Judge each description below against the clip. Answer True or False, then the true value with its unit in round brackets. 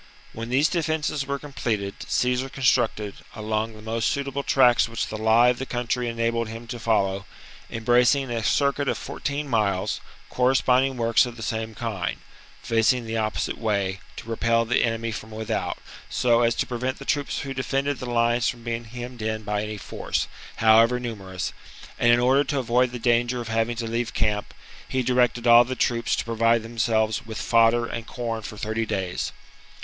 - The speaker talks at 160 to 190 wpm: True (180 wpm)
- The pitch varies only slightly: True (2.0 semitones)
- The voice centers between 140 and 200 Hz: False (115 Hz)